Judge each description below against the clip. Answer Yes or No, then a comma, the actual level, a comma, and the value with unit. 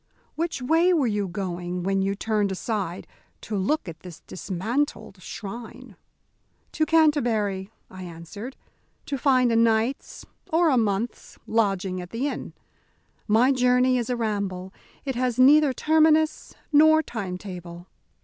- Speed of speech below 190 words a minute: Yes, average, 140 wpm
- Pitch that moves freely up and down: Yes, wide, 5.7 semitones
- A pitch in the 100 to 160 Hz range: No, high, 225 Hz